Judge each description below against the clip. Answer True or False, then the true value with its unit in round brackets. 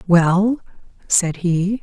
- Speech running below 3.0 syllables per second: True (2.5 syllables/s)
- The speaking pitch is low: False (185 Hz)